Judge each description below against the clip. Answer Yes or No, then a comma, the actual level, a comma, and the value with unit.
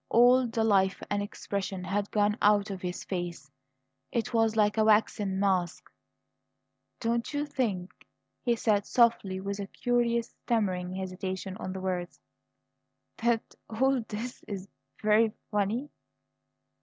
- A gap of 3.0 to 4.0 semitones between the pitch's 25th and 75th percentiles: Yes, average, 3.4 semitones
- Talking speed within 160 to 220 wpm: No, average, 145 wpm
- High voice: Yes, high, 205 Hz